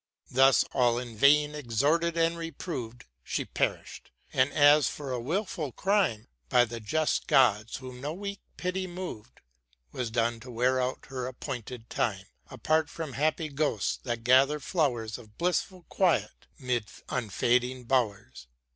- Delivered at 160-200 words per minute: No, average, 145 wpm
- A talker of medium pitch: No, low, 130 Hz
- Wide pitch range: No, average, 4.7 semitones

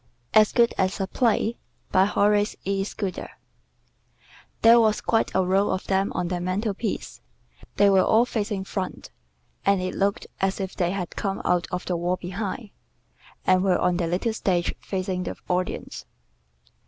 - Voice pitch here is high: Yes, high, 195 Hz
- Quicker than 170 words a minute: No, average, 165 wpm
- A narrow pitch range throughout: Yes, narrow, 2.1 semitones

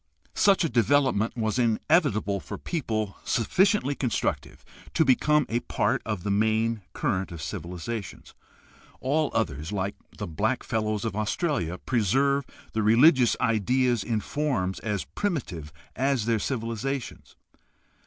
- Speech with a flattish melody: No, average, 4.7 semitones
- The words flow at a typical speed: No, slow, 125 wpm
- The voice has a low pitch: Yes, low, 115 Hz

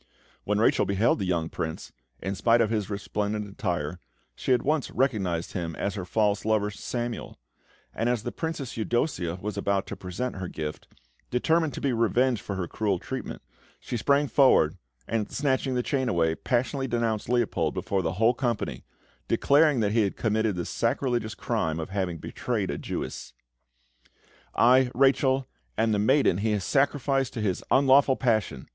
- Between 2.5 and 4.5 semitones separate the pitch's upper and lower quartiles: No, average, 4.9 semitones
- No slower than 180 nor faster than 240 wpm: No, average, 170 wpm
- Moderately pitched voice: No, low, 110 Hz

